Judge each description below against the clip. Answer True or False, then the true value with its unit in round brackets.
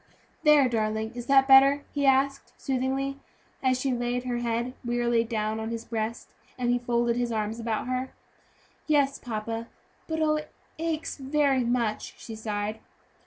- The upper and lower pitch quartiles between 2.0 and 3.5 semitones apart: True (3.0 semitones)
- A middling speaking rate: True (160 wpm)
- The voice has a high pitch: True (245 Hz)